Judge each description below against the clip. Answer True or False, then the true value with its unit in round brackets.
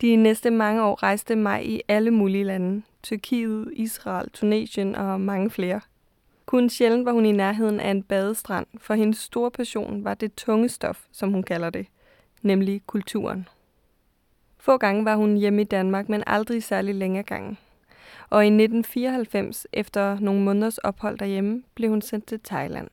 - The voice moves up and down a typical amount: False (2.1 semitones)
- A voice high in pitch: True (210 Hz)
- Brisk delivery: False (170 wpm)